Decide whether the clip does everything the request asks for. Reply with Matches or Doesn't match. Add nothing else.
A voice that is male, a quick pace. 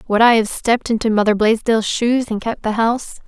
Doesn't match